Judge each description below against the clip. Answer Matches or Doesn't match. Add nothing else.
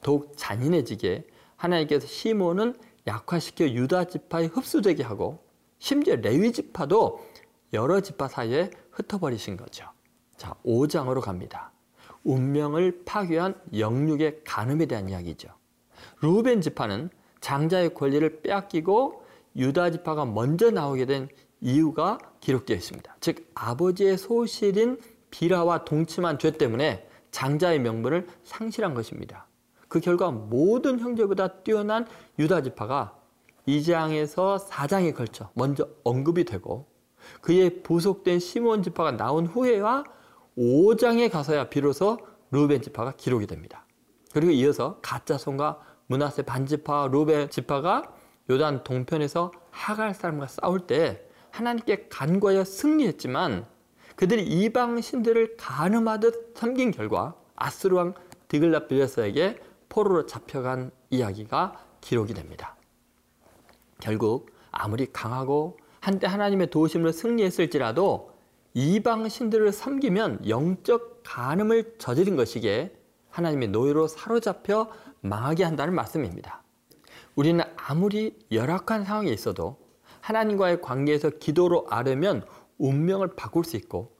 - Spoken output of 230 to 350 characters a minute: Matches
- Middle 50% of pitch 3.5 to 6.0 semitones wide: Doesn't match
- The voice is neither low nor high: Matches